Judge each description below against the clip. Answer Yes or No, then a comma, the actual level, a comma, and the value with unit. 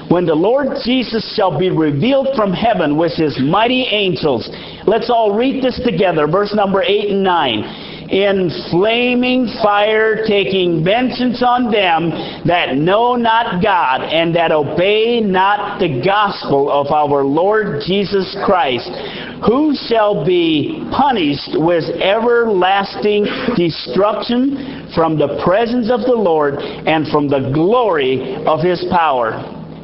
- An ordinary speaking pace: No, slow, 130 wpm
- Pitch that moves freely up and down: Yes, wide, 5.8 semitones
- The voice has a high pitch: Yes, high, 205 Hz